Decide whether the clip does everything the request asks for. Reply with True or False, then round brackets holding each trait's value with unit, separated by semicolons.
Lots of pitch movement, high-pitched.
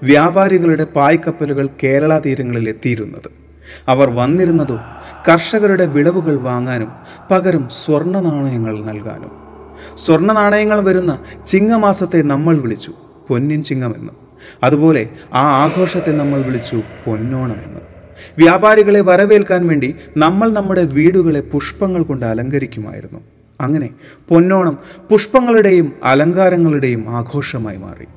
False (6.2 semitones; 150 Hz)